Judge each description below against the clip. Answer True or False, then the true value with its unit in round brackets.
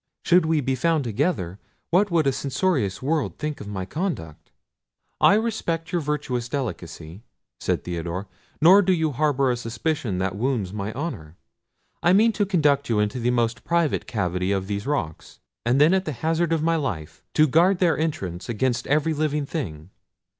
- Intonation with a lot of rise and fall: True (8.0 semitones)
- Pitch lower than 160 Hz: True (140 Hz)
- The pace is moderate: True (175 wpm)